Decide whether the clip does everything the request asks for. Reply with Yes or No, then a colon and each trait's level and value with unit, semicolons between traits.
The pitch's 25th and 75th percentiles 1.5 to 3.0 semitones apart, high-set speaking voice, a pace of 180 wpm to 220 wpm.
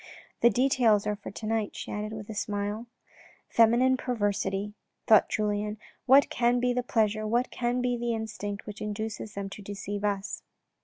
Yes: narrow, 2.6 semitones; high, 215 Hz; average, 190 wpm